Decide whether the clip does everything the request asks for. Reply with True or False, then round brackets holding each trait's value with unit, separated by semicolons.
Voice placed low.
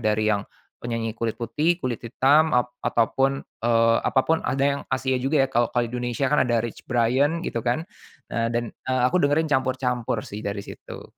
True (125 Hz)